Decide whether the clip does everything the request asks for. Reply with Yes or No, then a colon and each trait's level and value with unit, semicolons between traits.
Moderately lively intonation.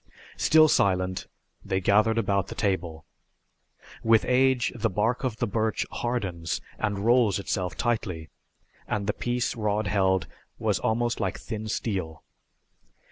Yes: average, 3.6 semitones